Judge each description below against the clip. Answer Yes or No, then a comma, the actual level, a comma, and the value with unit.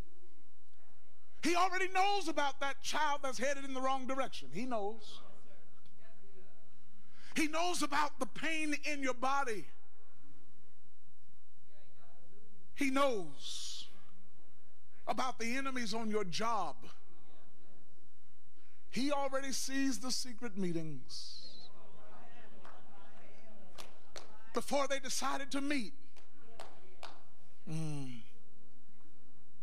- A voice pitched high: Yes, very high, 255 Hz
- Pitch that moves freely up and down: Yes, wide, 6.2 semitones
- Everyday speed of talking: No, slow, 85 wpm